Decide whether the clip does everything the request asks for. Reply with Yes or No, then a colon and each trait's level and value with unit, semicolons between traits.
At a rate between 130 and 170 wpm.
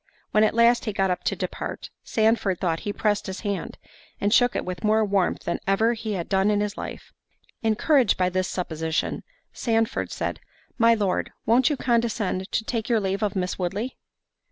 No: average, 190 wpm